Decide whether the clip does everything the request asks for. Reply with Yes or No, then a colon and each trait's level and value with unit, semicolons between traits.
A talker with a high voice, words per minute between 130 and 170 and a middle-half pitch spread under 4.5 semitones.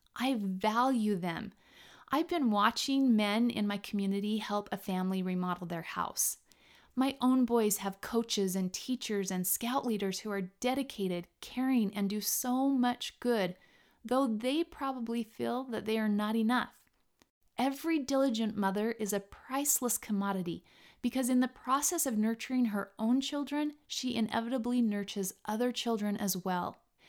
Yes: high, 230 Hz; average, 150 wpm; average, 4.1 semitones